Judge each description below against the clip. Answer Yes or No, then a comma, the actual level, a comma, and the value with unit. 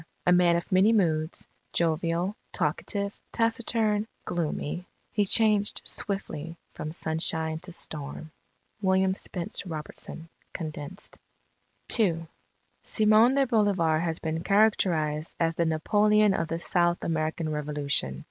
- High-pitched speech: No, medium, 170 Hz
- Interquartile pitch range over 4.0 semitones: Yes, average, 4.4 semitones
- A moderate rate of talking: No, slow, 115 wpm